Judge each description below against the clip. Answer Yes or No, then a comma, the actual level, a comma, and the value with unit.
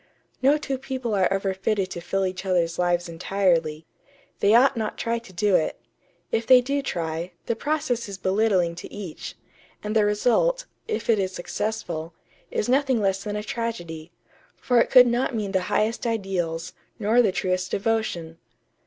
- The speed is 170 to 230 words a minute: Yes, average, 175 wpm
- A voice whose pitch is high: Yes, high, 205 Hz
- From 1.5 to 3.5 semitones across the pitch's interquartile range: No, average, 4.4 semitones